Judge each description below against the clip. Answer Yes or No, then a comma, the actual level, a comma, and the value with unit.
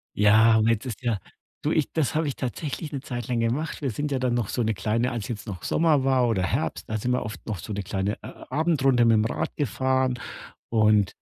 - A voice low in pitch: Yes, low, 120 Hz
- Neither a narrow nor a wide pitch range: Yes, average, 3.7 semitones